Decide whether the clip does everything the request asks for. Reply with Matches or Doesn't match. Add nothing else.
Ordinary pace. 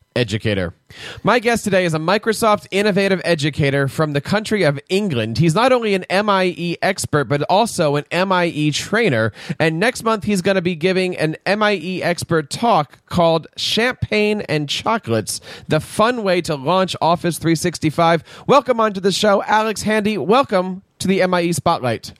Matches